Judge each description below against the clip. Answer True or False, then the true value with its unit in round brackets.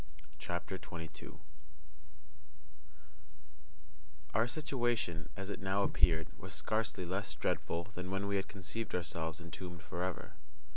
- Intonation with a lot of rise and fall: False (3.0 semitones)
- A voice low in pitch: True (90 Hz)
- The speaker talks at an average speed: False (110 wpm)